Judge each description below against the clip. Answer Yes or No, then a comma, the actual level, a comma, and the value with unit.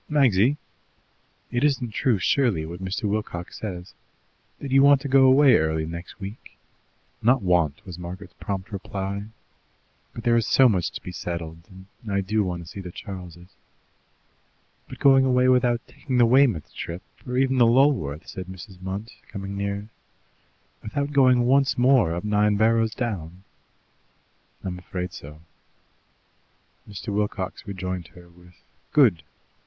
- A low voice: Yes, low, 100 Hz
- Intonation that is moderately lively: No, wide, 5.7 semitones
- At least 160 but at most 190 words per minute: No, average, 150 wpm